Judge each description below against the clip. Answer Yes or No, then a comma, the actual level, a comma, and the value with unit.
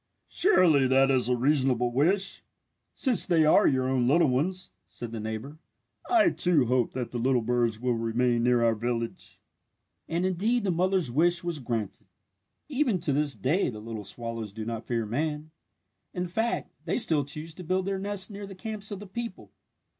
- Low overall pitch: No, medium, 145 Hz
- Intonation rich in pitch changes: Yes, wide, 7.4 semitones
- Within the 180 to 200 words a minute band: Yes, average, 185 wpm